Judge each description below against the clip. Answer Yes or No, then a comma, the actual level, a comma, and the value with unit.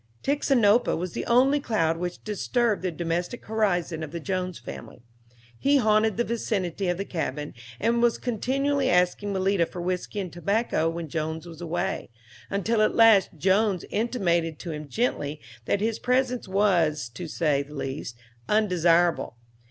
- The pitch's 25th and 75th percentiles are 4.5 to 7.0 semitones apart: Yes, average, 5.0 semitones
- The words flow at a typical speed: Yes, average, 155 wpm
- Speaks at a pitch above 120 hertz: Yes, medium, 185 Hz